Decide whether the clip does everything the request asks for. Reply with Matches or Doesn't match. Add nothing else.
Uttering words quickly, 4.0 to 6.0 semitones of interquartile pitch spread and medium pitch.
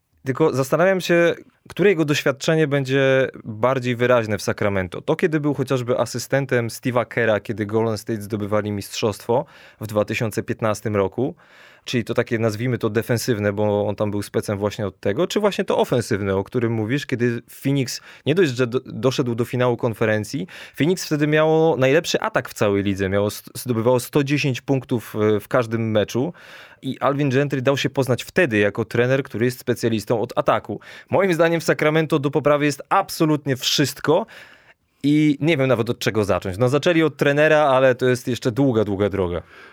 Doesn't match